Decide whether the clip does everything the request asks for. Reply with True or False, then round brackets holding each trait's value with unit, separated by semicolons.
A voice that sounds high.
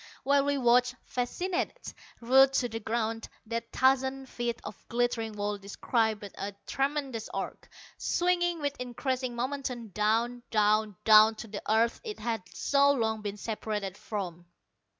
True (235 Hz)